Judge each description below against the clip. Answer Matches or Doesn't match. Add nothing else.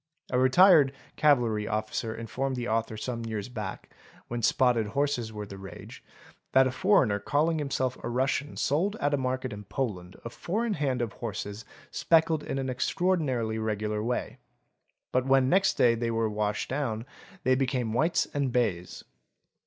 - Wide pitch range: Doesn't match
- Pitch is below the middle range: Matches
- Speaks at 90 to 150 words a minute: Doesn't match